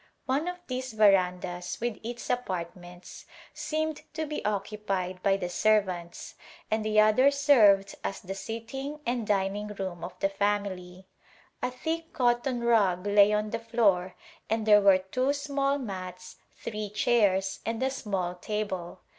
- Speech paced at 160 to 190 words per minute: No, average, 145 wpm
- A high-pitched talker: Yes, high, 210 Hz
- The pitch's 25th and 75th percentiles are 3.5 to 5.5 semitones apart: Yes, average, 4.3 semitones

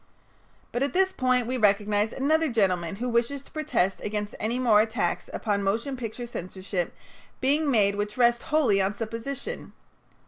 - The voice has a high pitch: Yes, high, 230 Hz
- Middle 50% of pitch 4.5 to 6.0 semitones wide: No, average, 4.0 semitones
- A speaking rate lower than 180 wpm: Yes, average, 160 wpm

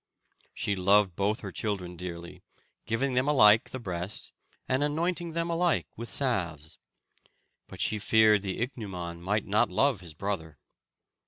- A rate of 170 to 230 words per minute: No, average, 145 wpm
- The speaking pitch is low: Yes, low, 105 Hz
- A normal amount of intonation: No, wide, 5.9 semitones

